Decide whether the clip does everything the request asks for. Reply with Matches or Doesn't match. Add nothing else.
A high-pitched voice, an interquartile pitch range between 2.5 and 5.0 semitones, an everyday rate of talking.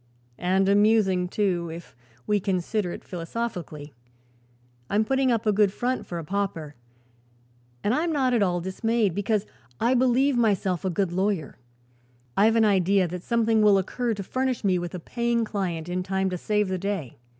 Matches